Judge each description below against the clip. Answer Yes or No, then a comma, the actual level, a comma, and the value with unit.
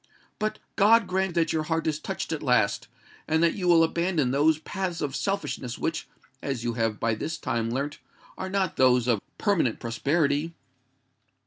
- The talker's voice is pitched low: No, medium, 155 Hz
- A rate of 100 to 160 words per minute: No, average, 175 wpm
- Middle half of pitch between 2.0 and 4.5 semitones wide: No, wide, 5.5 semitones